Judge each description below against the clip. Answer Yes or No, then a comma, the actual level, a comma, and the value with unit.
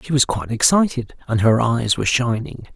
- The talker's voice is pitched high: No, low, 120 Hz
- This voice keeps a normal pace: Yes, average, 195 wpm